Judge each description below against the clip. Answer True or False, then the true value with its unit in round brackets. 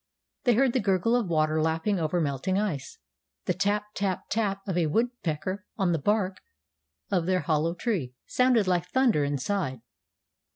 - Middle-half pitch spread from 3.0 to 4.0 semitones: False (4.7 semitones)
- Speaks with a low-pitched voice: False (185 Hz)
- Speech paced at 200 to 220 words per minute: False (160 wpm)